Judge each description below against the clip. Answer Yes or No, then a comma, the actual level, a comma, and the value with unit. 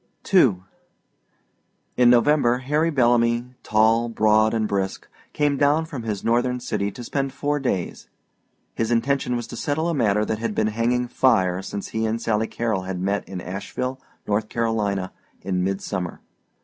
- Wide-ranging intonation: No, average, 3.7 semitones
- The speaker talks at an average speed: Yes, average, 160 wpm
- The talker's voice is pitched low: Yes, low, 115 Hz